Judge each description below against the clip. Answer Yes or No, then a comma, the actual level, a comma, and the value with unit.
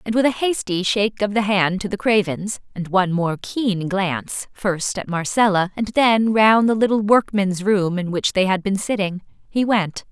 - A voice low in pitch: No, high, 200 Hz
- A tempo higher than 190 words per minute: Yes, average, 200 wpm